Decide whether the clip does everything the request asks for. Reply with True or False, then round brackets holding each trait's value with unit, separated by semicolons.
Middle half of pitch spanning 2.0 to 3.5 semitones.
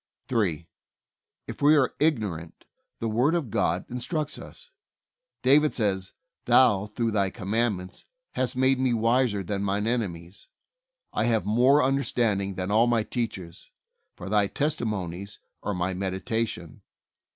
False (4.6 semitones)